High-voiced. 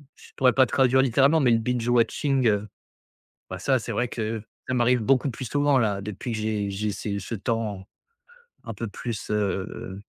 No: low, 115 Hz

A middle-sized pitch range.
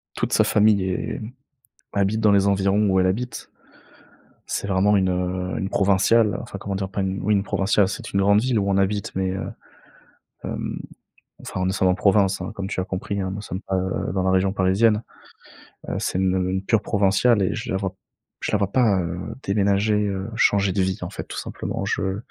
No: narrow, 1.5 semitones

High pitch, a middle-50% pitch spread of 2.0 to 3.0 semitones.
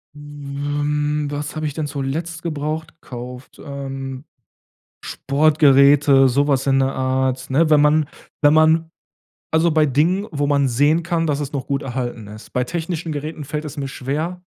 No: medium, 145 Hz; narrow, 2.4 semitones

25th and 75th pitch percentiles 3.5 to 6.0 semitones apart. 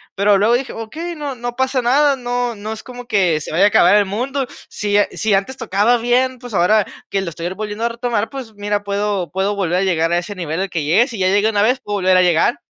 Yes: average, 4.1 semitones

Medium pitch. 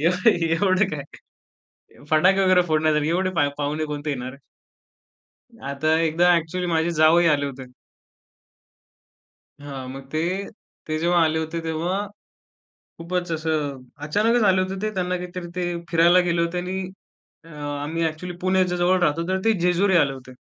Yes: medium, 165 Hz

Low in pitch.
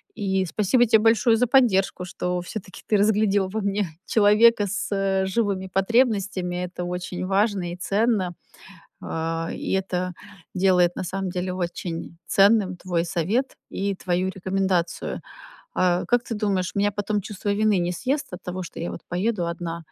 No: high, 190 Hz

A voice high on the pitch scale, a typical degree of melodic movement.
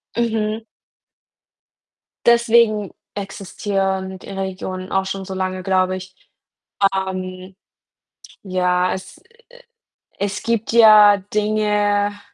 No: high, 195 Hz; narrow, 2.1 semitones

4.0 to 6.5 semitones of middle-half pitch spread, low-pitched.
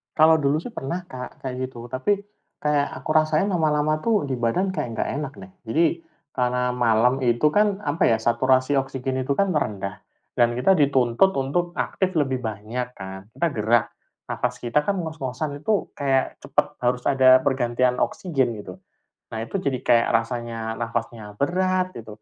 Yes: average, 4.8 semitones; low, 130 Hz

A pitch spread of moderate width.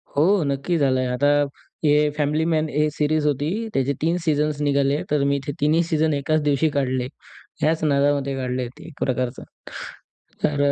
No: narrow, 1.9 semitones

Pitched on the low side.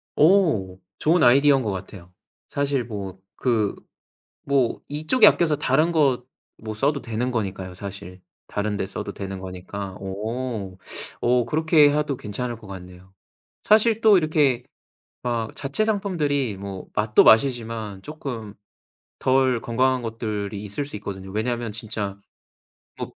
Yes: low, 115 Hz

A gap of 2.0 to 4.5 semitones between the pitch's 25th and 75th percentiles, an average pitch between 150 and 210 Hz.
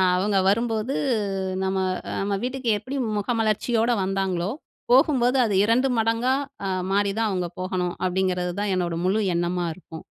Yes: average, 3.8 semitones; high, 205 Hz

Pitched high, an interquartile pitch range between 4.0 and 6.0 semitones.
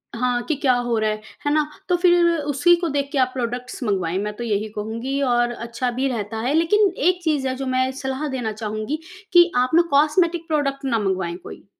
Yes: very high, 260 Hz; average, 4.7 semitones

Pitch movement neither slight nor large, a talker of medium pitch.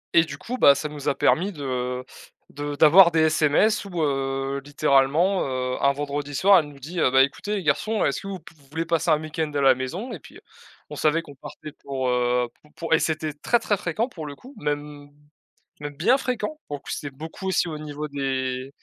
Yes: average, 3.2 semitones; medium, 150 Hz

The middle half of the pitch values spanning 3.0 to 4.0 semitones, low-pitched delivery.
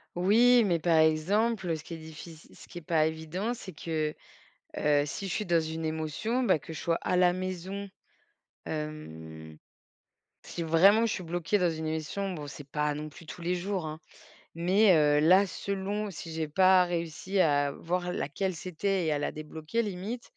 No: average, 3.6 semitones; medium, 170 Hz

